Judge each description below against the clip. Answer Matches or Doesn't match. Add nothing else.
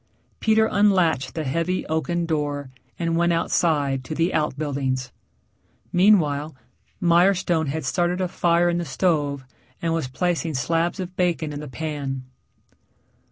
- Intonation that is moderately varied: Matches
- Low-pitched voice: Doesn't match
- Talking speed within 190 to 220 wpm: Doesn't match